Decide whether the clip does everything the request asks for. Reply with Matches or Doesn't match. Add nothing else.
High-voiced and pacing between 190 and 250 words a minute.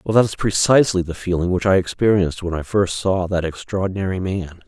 Doesn't match